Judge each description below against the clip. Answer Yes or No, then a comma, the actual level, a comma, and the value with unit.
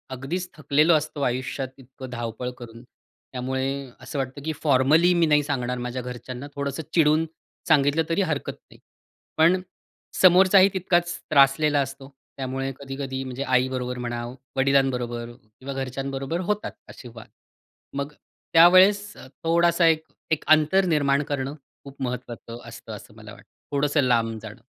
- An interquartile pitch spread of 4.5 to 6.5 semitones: No, average, 3.7 semitones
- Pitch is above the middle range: No, medium, 140 Hz